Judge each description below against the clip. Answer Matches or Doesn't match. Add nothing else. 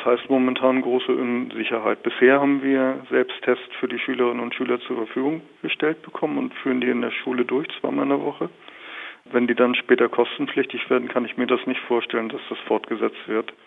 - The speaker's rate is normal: Doesn't match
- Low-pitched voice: Matches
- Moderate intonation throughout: Doesn't match